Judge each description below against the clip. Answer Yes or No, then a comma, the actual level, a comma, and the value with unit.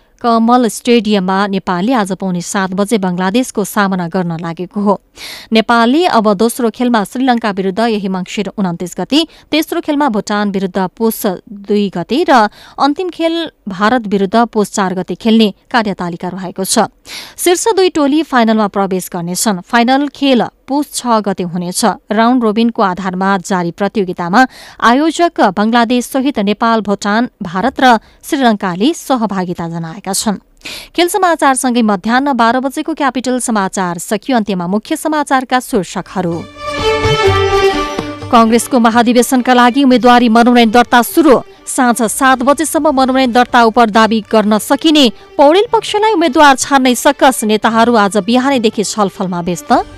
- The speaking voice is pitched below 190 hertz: No, high, 230 Hz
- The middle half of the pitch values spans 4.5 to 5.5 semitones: Yes, average, 4.9 semitones